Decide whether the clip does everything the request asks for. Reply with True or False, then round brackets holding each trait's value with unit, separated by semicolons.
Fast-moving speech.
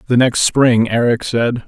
False (180 wpm)